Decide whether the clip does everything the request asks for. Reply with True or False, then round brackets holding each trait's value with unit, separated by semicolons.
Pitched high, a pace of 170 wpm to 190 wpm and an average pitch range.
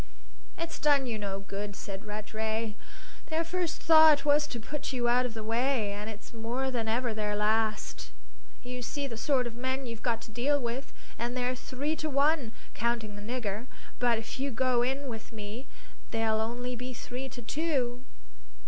True (240 Hz; 185 wpm; 3.3 semitones)